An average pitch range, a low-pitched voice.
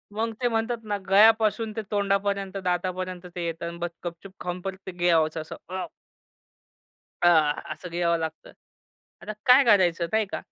No: average, 3.5 semitones; medium, 185 Hz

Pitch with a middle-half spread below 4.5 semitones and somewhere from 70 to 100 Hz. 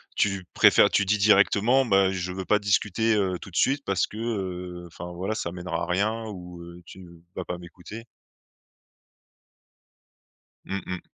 Yes: average, 2.9 semitones; very low, 95 Hz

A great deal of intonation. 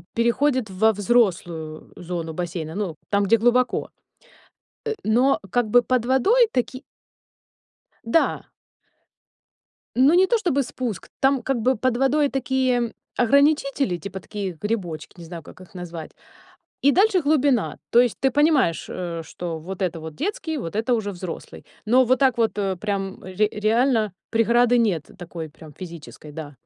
Yes: wide, 6.5 semitones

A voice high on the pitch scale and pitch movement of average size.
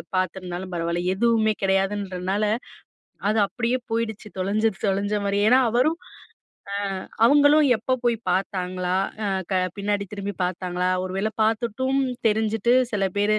Yes: high, 205 Hz; average, 3.3 semitones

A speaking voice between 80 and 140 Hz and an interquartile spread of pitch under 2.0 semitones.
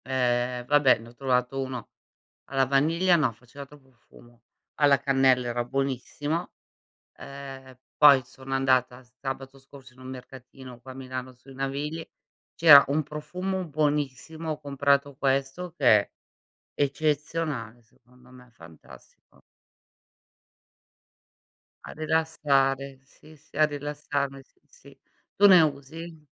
No: low, 135 Hz; narrow, 2.5 semitones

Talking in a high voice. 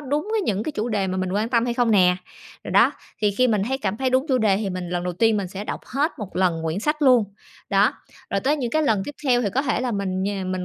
Yes: high, 215 Hz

